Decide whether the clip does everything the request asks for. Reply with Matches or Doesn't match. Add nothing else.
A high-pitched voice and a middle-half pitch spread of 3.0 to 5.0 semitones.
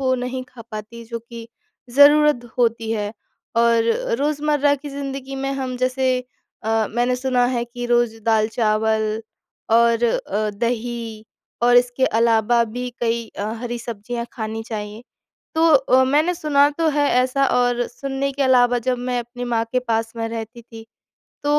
Doesn't match